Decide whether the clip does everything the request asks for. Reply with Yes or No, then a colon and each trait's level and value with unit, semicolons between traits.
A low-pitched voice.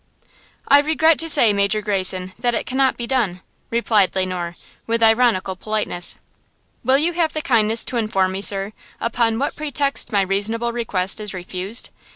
No: high, 220 Hz